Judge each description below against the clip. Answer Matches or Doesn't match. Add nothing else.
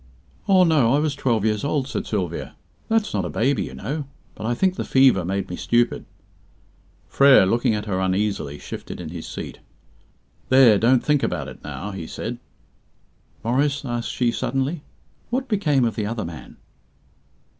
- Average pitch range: Doesn't match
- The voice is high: Doesn't match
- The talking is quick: Doesn't match